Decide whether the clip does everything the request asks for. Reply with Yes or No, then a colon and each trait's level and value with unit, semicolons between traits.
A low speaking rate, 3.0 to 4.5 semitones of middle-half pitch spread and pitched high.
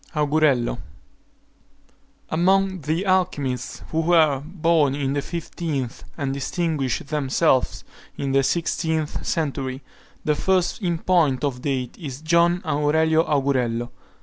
No: slow, 115 wpm; average, 3.7 semitones; medium, 150 Hz